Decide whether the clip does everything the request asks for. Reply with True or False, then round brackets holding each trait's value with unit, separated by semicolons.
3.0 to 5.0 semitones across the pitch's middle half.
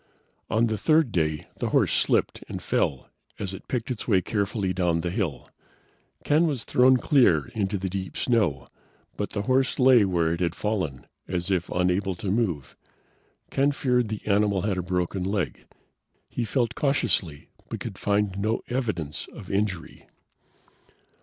True (4.6 semitones)